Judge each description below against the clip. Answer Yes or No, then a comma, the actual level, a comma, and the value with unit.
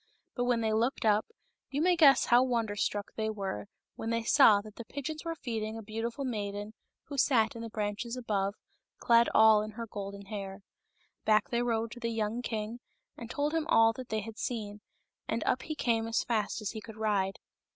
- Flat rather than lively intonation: Yes, narrow, 2.2 semitones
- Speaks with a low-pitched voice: No, high, 225 Hz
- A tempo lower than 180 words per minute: No, fast, 205 wpm